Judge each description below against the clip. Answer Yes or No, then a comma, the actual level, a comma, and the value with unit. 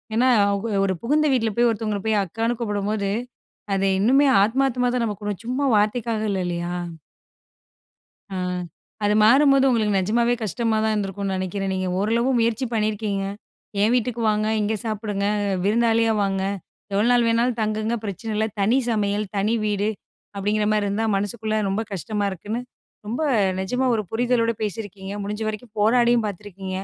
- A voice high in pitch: Yes, high, 215 Hz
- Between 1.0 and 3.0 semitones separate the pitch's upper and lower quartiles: Yes, narrow, 2.5 semitones